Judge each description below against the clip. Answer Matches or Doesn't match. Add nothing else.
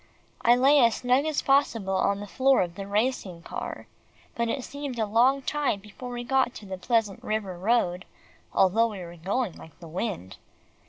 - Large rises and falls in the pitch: Doesn't match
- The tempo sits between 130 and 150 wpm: Doesn't match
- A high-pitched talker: Matches